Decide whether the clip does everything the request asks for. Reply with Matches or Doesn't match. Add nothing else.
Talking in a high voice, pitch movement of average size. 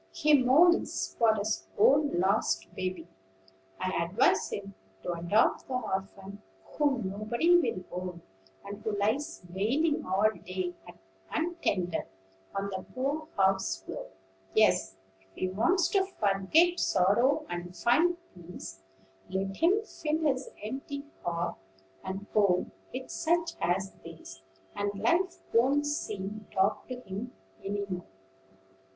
Doesn't match